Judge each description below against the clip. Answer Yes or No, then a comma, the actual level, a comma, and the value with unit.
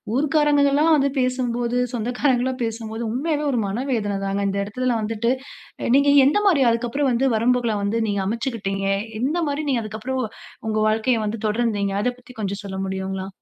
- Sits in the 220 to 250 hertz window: Yes, high, 235 Hz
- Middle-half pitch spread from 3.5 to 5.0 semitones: Yes, average, 4.1 semitones